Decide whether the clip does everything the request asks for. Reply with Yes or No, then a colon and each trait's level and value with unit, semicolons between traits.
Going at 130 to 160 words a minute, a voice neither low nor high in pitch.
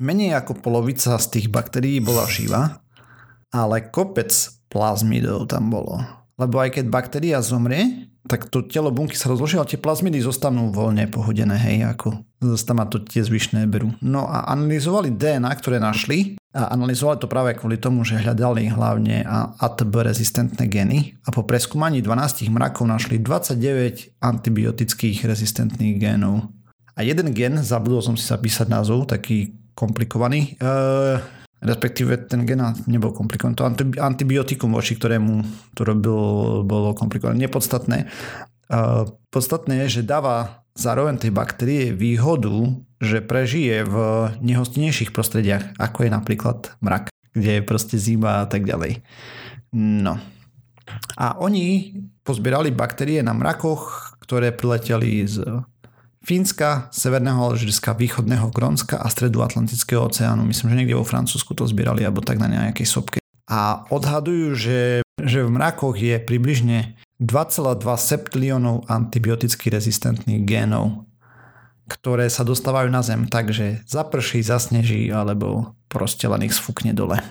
No: average, 135 wpm; low, 120 Hz